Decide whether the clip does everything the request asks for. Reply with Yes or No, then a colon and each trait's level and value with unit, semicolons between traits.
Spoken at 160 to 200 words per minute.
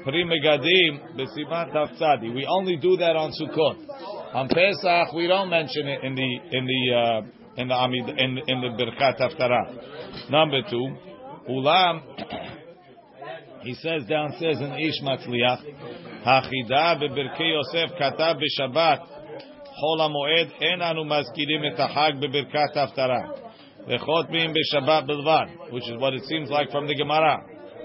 No: average, 140 wpm